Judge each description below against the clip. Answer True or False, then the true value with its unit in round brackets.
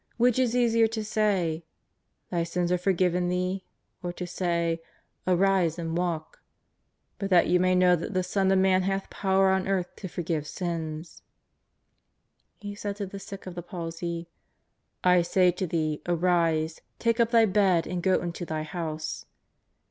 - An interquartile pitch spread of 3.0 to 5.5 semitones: False (2.4 semitones)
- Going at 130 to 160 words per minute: False (175 wpm)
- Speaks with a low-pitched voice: False (180 Hz)